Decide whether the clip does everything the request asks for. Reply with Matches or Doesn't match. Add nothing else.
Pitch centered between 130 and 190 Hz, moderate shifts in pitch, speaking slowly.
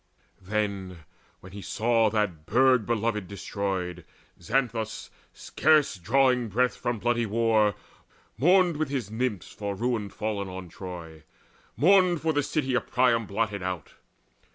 Doesn't match